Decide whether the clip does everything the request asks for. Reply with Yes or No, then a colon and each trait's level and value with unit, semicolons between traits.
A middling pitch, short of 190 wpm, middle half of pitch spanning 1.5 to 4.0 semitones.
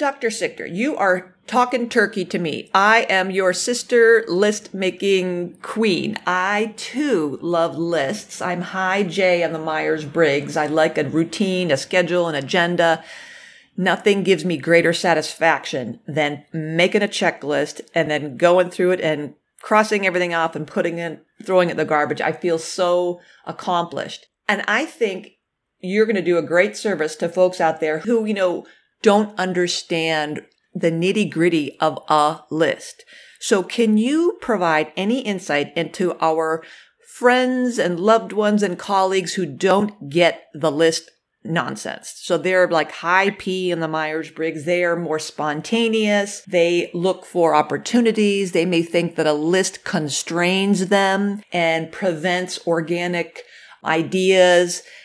Yes: medium, 180 Hz; average, 150 wpm; average, 3.6 semitones